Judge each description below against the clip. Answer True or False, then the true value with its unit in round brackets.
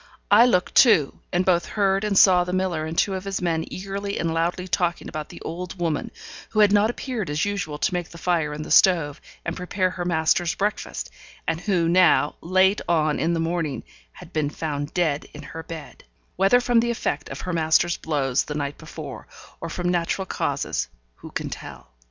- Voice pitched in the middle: True (175 Hz)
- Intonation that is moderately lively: True (3.2 semitones)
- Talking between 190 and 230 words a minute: True (200 wpm)